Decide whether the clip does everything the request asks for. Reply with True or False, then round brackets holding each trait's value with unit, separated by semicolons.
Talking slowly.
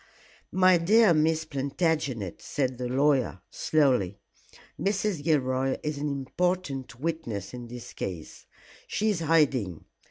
True (120 wpm)